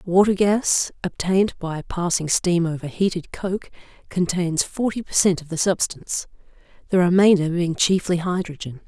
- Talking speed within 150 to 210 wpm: No, average, 140 wpm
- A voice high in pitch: No, medium, 180 Hz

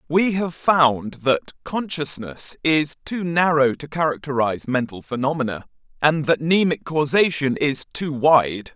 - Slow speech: Yes, slow, 130 wpm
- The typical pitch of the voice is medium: Yes, medium, 145 Hz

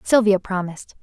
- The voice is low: No, high, 200 Hz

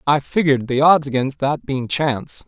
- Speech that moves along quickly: No, average, 195 wpm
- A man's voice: Yes, male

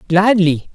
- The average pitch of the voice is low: No, medium, 185 Hz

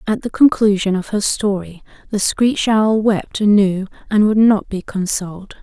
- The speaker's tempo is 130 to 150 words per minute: No, average, 170 wpm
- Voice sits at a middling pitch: No, high, 205 Hz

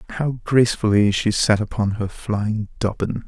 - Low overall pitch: Yes, low, 110 Hz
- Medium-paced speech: Yes, average, 145 wpm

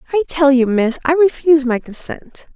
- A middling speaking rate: Yes, average, 190 wpm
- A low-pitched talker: No, very high, 285 Hz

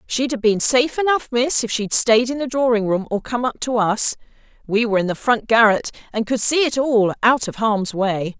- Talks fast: Yes, fast, 235 wpm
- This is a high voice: Yes, high, 230 Hz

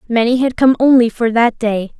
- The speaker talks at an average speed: No, fast, 210 wpm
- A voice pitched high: Yes, high, 235 Hz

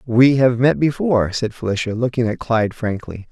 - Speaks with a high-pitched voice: No, low, 120 Hz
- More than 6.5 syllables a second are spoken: No, 5.4 syllables/s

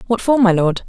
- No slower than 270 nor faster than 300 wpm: Yes, fast, 275 wpm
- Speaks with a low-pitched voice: No, high, 205 Hz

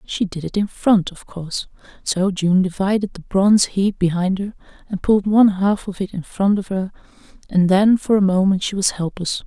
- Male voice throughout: No, female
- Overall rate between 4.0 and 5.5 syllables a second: Yes, 5.2 syllables/s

